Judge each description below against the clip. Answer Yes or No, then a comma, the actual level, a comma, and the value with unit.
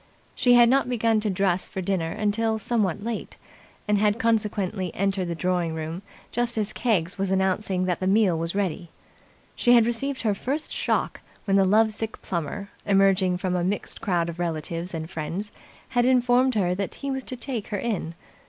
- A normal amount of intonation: Yes, average, 4.0 semitones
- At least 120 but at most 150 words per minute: No, average, 190 wpm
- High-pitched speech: Yes, high, 200 Hz